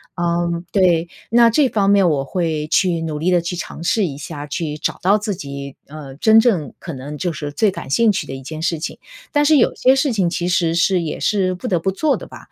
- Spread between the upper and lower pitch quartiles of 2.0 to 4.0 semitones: No, average, 4.7 semitones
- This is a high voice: No, medium, 175 Hz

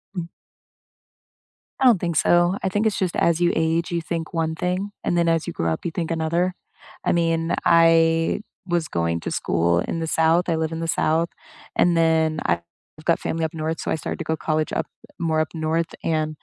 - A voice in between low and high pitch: Yes, medium, 165 Hz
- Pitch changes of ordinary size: No, narrow, 1.3 semitones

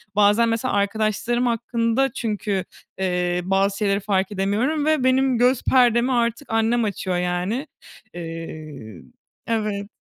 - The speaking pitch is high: Yes, high, 215 Hz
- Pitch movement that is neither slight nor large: Yes, average, 3.9 semitones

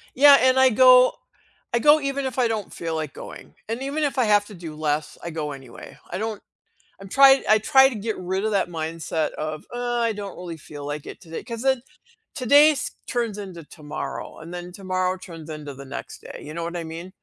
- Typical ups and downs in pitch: No, wide, 7.4 semitones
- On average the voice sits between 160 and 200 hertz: Yes, high, 190 Hz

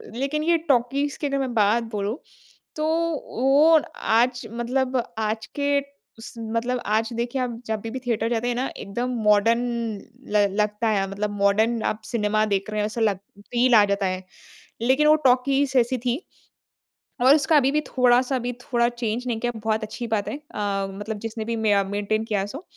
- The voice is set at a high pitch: Yes, high, 235 Hz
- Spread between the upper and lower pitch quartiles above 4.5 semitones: No, average, 3.2 semitones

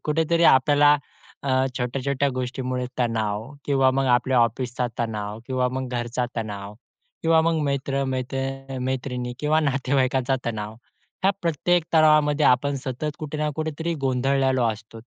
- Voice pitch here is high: No, low, 130 Hz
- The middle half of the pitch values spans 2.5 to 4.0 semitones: Yes, average, 2.9 semitones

